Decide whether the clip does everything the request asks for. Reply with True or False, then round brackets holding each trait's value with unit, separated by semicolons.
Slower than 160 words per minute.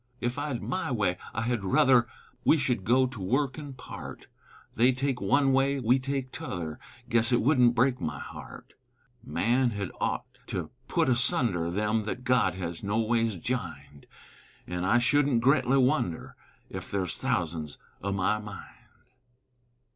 True (150 wpm)